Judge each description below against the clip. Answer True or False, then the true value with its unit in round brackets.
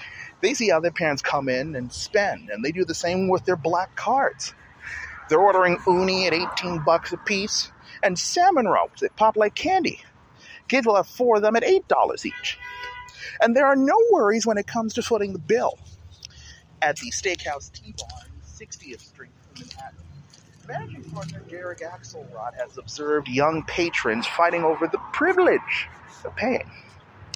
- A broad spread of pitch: True (8.8 semitones)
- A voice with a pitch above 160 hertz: True (185 Hz)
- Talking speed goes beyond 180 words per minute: False (165 wpm)